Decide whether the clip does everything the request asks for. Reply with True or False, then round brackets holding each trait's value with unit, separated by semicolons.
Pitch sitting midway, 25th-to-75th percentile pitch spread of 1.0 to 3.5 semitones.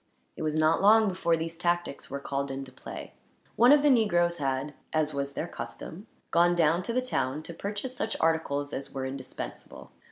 False (165 Hz; 5.4 semitones)